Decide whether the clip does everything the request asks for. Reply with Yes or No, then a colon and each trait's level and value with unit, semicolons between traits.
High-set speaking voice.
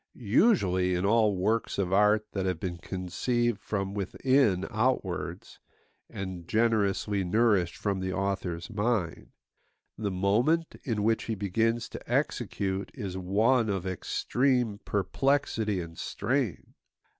No: low, 100 Hz